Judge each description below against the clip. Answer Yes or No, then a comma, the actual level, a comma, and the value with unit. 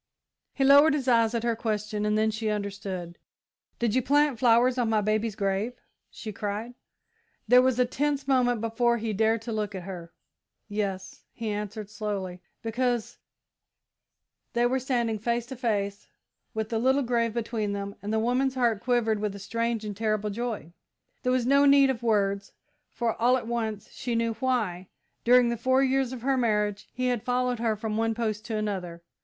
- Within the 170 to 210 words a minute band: Yes, average, 185 wpm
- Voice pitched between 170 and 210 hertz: No, high, 225 Hz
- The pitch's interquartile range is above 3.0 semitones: No, average, 2.7 semitones